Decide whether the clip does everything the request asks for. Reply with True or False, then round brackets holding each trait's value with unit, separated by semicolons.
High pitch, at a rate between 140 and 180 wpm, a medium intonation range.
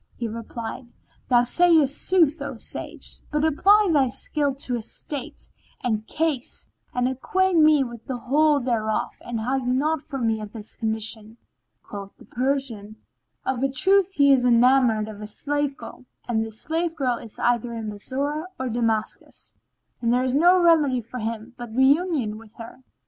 True (255 Hz; 170 wpm; 4.3 semitones)